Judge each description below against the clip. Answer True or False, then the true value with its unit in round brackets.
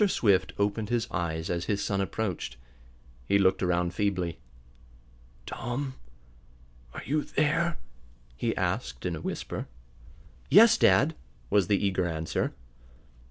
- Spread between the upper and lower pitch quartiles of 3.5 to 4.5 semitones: False (5.6 semitones)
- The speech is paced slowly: True (120 wpm)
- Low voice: True (100 Hz)